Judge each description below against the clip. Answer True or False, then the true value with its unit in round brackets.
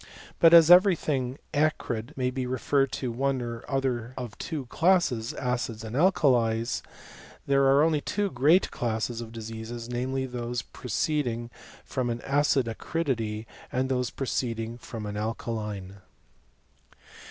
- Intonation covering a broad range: False (3.2 semitones)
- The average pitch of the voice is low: True (125 Hz)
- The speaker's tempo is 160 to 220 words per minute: False (140 wpm)